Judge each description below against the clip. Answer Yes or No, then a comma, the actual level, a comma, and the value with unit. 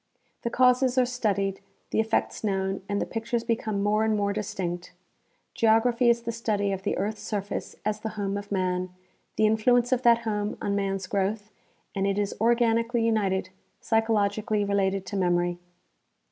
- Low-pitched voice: No, high, 210 Hz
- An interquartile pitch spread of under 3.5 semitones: Yes, narrow, 2.6 semitones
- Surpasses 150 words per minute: Yes, average, 170 wpm